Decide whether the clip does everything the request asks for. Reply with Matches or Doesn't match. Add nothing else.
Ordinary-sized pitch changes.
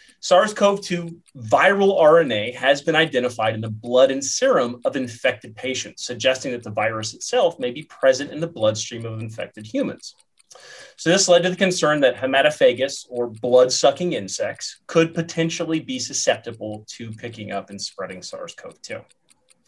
Doesn't match